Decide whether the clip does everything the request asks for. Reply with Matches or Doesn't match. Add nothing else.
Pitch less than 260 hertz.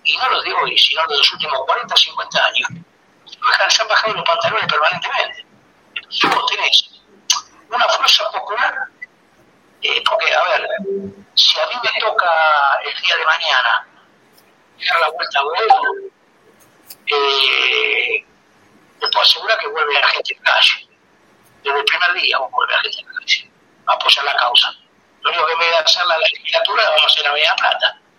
Doesn't match